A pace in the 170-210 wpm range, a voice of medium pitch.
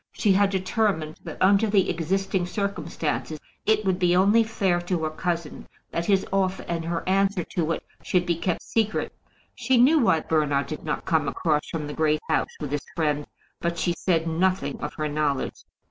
Yes: average, 190 wpm; medium, 175 Hz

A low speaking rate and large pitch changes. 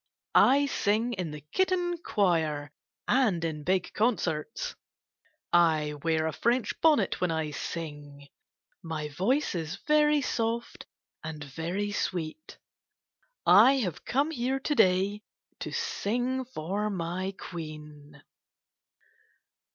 Yes: slow, 110 wpm; wide, 7.7 semitones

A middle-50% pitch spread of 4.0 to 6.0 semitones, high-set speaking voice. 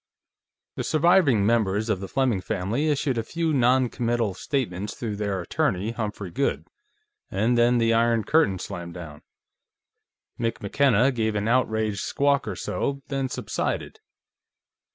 No: average, 4.5 semitones; low, 115 Hz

